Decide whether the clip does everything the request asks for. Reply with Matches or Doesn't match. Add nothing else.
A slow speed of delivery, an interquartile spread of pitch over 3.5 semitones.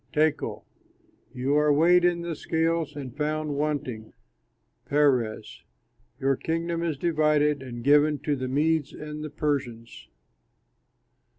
Doesn't match